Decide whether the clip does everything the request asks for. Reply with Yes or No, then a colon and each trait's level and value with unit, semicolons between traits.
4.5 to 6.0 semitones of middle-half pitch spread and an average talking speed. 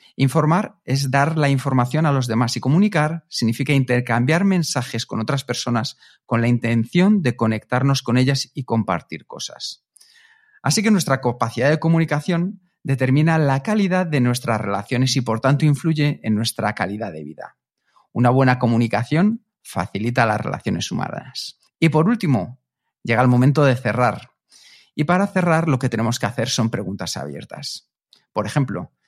Yes: wide, 5.5 semitones; average, 155 wpm